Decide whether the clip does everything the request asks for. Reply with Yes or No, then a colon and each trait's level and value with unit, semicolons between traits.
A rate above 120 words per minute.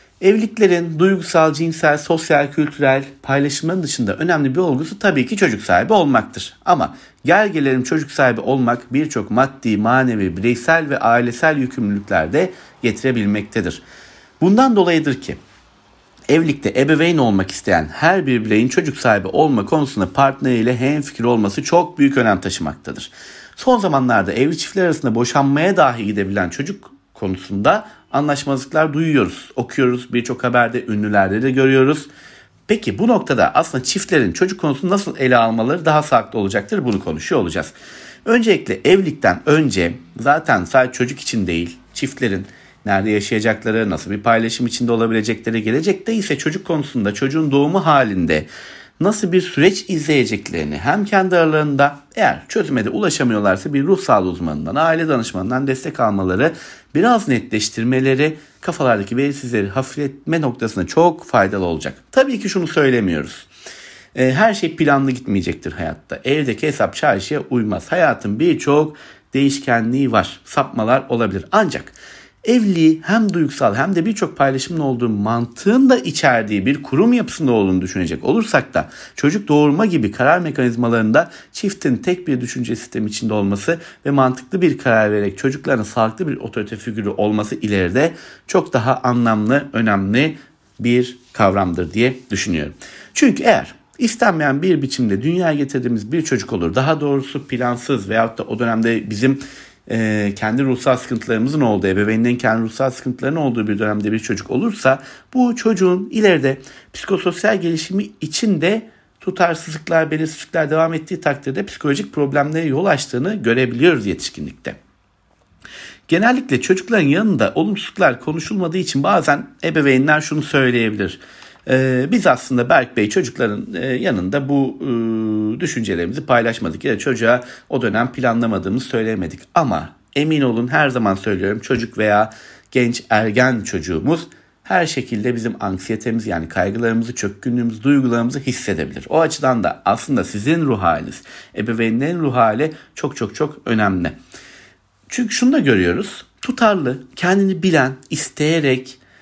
Yes: average, 130 wpm